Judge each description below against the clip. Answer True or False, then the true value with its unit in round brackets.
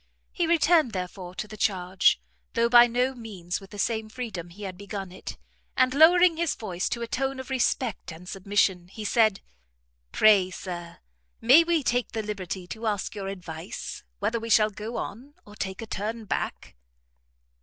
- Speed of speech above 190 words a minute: False (175 wpm)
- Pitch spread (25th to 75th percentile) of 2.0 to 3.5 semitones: False (4.4 semitones)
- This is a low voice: False (215 Hz)